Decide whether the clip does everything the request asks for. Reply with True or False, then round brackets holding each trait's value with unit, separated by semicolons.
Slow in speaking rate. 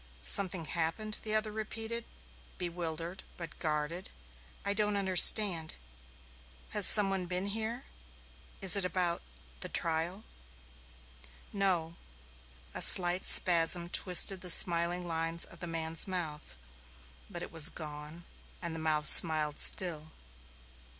True (120 wpm)